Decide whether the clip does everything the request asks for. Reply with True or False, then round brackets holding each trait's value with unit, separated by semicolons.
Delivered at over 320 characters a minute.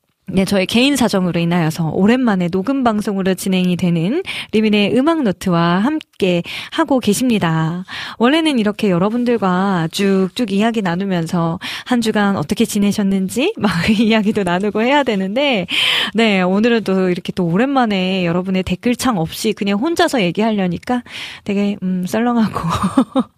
True (330 characters per minute)